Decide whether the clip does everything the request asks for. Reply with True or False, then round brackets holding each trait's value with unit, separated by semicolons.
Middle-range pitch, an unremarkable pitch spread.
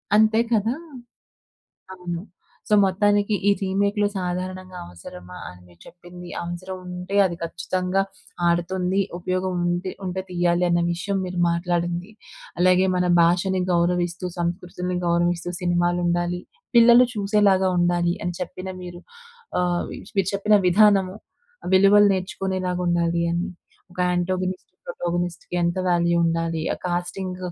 False (180 Hz; 1.5 semitones)